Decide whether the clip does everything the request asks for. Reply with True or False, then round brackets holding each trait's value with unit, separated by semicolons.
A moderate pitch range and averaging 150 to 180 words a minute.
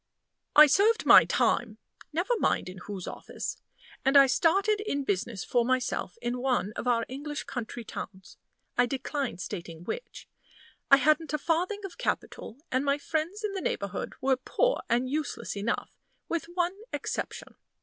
False (6.1 semitones; 160 wpm)